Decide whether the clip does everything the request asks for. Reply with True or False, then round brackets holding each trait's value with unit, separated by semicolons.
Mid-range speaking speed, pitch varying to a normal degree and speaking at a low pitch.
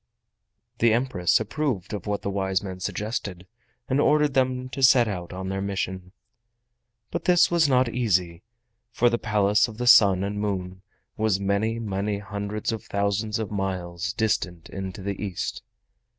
True (160 wpm; 3.4 semitones; 100 Hz)